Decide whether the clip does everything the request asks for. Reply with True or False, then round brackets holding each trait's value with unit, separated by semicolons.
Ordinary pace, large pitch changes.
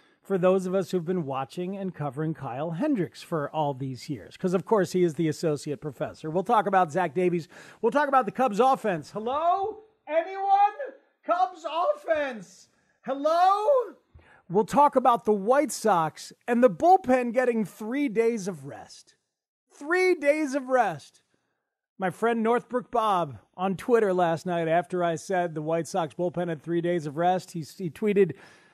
True (165 wpm; 7.9 semitones)